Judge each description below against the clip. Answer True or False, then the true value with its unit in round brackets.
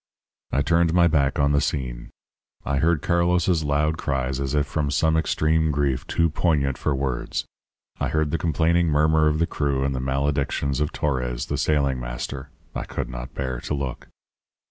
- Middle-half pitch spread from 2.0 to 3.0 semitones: True (2.7 semitones)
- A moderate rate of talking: True (180 wpm)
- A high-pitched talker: False (70 Hz)